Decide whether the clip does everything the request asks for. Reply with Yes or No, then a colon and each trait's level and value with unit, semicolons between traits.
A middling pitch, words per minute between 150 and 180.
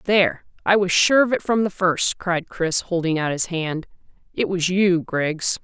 No: medium, 180 Hz; average, 200 wpm